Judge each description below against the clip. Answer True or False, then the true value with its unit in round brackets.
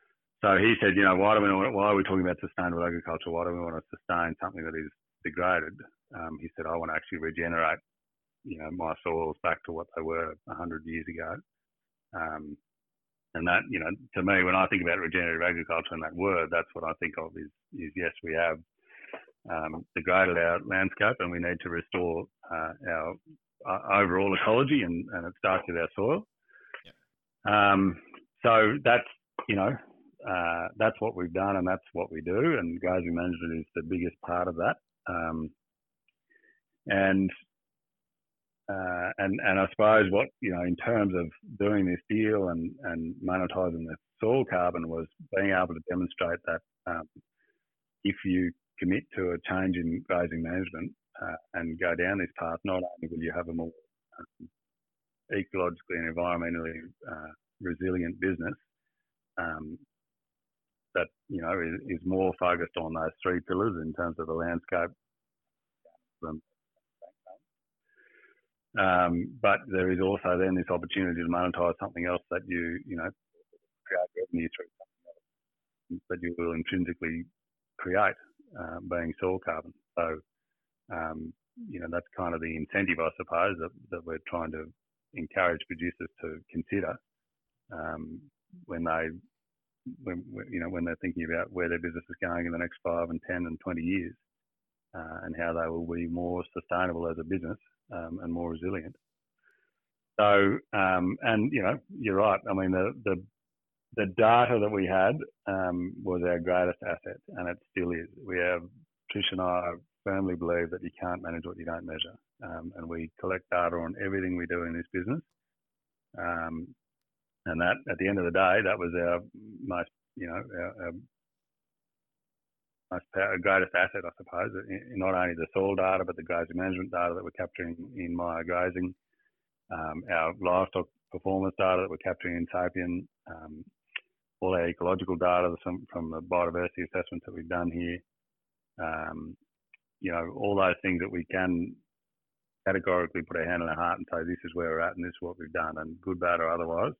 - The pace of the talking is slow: False (175 wpm)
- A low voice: True (90 Hz)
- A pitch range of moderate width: False (1.9 semitones)